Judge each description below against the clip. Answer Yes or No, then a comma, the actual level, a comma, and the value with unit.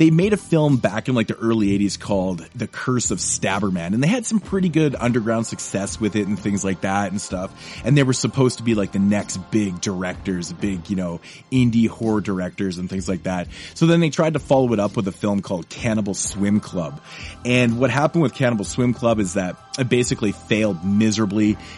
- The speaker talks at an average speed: No, fast, 220 wpm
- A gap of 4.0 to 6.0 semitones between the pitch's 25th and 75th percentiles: Yes, average, 4.4 semitones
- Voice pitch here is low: Yes, low, 110 Hz